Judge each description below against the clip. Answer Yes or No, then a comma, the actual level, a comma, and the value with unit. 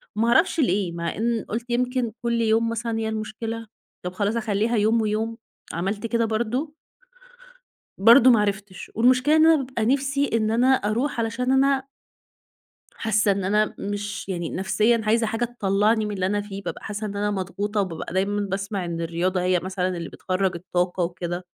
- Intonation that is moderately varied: Yes, average, 3.2 semitones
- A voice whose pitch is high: Yes, high, 215 Hz